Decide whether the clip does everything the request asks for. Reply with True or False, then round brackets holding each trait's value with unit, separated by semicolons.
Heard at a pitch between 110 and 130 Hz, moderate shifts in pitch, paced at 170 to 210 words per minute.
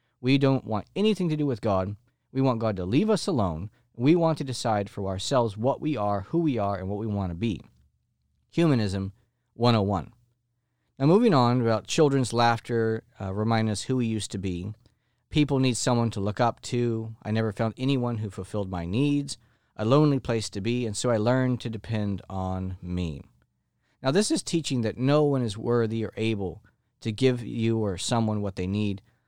True (115 Hz; 3.8 semitones; 195 wpm)